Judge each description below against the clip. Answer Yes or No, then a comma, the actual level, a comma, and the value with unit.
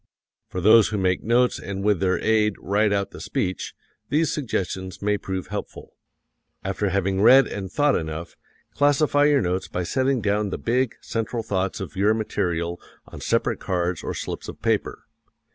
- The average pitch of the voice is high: No, low, 100 Hz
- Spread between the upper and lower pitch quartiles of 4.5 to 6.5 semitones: No, average, 3.7 semitones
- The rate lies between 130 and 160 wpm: No, average, 170 wpm